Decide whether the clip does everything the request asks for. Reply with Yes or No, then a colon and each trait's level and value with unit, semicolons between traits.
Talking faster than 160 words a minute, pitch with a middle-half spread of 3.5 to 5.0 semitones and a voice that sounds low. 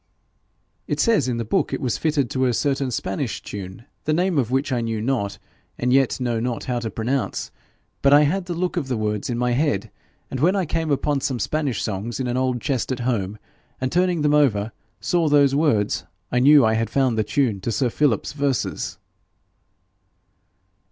Yes: average, 200 wpm; average, 4.2 semitones; low, 130 Hz